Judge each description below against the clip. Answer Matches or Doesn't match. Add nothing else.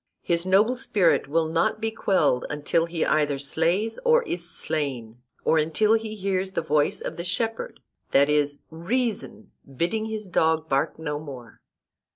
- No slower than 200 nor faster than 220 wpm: Doesn't match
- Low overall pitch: Doesn't match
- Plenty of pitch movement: Matches